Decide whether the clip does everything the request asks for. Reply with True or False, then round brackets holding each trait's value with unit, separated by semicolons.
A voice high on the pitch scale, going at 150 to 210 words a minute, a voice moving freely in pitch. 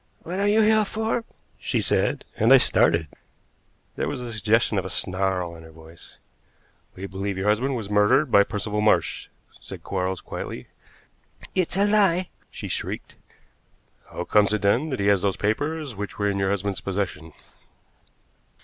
False (105 Hz; 165 wpm; 7.1 semitones)